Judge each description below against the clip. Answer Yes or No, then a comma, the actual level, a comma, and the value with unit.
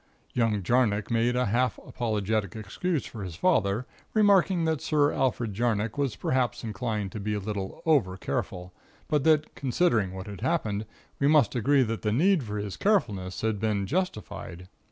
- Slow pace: No, average, 170 wpm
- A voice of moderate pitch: No, low, 115 Hz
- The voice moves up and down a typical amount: No, wide, 5.7 semitones